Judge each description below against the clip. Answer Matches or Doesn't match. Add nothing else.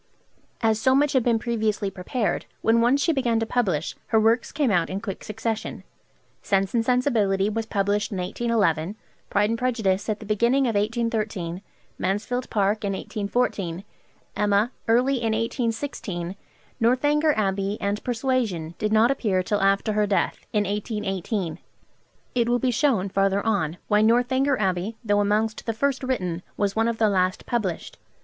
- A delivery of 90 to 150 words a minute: Doesn't match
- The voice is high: Matches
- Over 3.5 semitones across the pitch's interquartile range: Doesn't match